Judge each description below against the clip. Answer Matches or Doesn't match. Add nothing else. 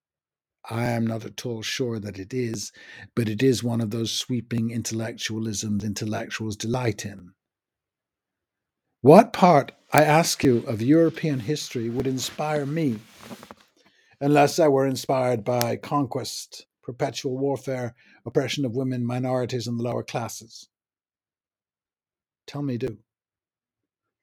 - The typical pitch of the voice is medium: Doesn't match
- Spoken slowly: Matches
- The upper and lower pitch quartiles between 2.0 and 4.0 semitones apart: Matches